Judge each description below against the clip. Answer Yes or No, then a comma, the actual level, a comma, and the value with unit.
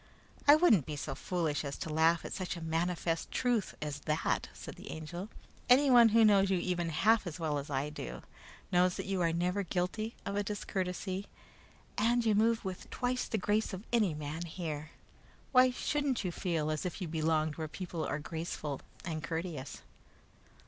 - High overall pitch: No, medium, 180 Hz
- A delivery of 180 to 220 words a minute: Yes, average, 185 wpm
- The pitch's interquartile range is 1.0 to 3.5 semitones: No, average, 4.7 semitones